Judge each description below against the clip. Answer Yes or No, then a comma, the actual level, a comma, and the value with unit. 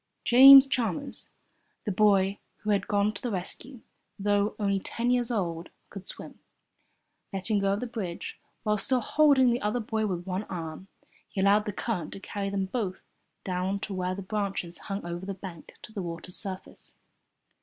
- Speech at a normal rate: Yes, average, 175 wpm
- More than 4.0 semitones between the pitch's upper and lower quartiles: No, narrow, 2.6 semitones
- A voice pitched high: Yes, high, 200 Hz